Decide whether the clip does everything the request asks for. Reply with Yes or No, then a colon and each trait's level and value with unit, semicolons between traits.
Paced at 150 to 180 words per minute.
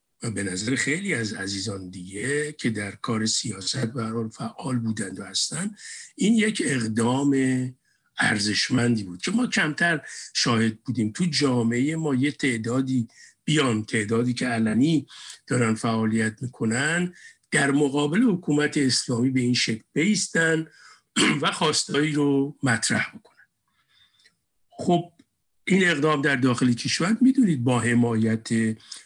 No: average, 125 wpm